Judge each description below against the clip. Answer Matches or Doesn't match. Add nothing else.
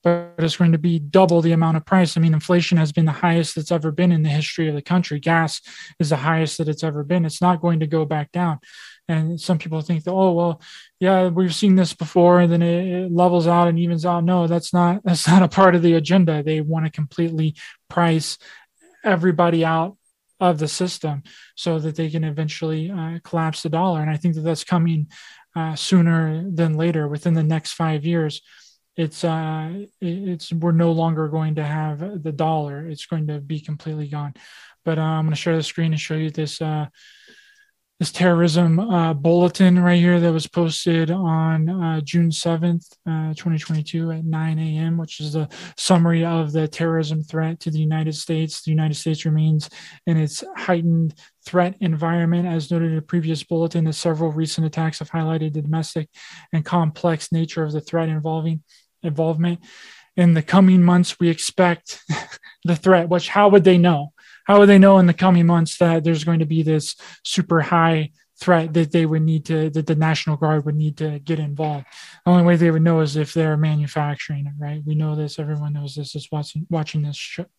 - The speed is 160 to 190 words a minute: Doesn't match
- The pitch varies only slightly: Matches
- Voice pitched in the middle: Matches